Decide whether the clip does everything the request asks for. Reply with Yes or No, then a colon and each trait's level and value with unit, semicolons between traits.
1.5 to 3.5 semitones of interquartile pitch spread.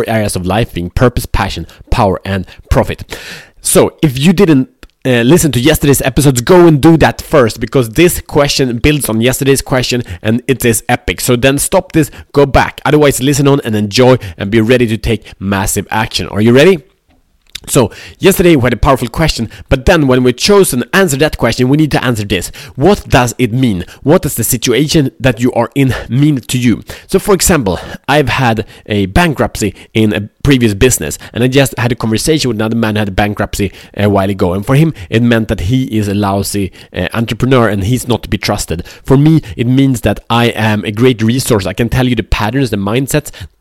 No: average, 4.7 semitones